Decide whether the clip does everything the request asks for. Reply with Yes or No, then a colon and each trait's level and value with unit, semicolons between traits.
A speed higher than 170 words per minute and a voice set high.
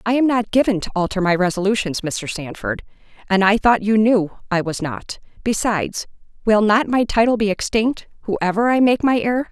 Yes: average, 190 wpm; high, 210 Hz